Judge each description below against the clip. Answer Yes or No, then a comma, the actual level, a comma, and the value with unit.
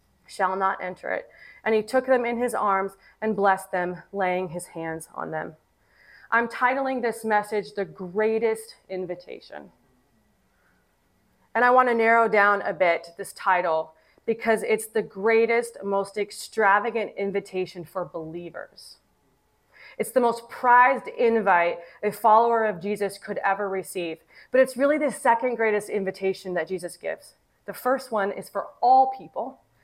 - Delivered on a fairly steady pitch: No, average, 3.7 semitones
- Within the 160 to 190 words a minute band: No, average, 150 wpm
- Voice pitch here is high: Yes, high, 205 Hz